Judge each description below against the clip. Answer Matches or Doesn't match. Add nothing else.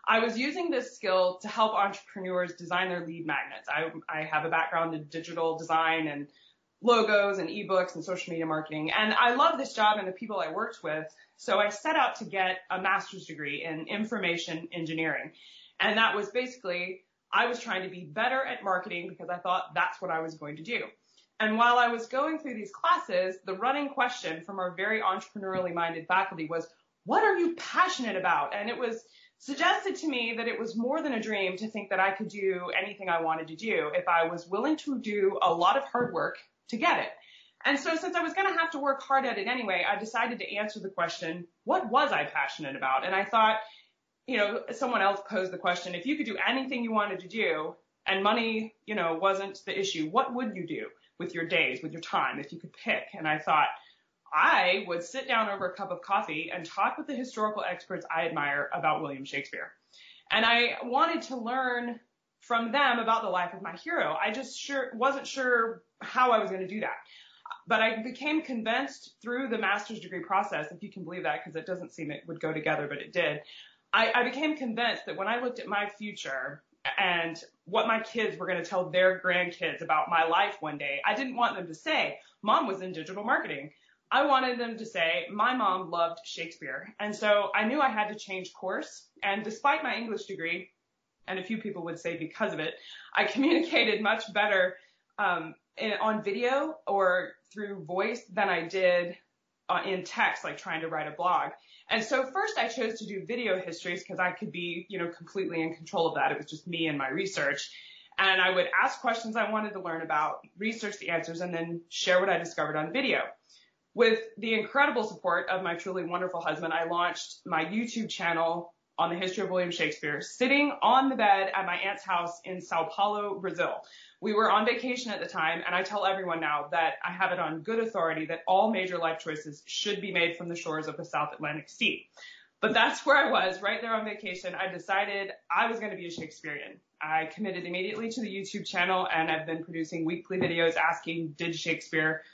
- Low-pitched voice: Doesn't match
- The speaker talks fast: Matches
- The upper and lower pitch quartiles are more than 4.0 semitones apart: Matches